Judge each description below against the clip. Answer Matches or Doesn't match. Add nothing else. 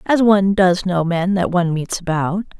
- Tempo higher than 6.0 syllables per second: Doesn't match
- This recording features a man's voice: Doesn't match